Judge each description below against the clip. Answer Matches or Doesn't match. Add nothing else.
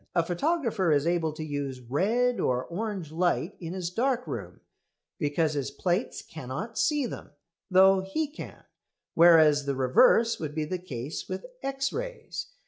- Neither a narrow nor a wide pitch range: Doesn't match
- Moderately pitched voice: Matches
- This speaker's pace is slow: Doesn't match